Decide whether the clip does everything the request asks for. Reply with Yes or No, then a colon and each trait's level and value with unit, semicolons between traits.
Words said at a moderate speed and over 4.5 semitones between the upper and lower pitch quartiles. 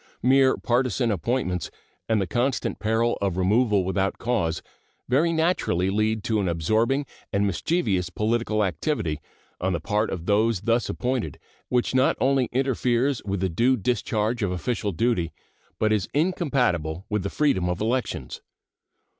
Yes: average, 145 wpm; average, 4.9 semitones